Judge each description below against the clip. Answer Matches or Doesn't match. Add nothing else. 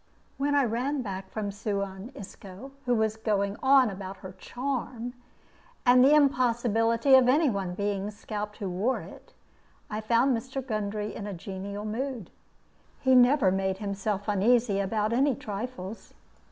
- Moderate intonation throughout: Matches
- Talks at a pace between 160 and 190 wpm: Doesn't match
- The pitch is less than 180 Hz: Doesn't match